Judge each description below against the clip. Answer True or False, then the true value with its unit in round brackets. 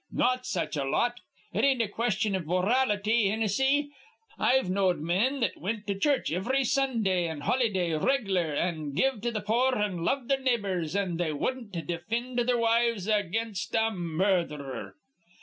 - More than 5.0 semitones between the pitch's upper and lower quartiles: True (5.4 semitones)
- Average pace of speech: True (160 wpm)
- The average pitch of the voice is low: False (210 Hz)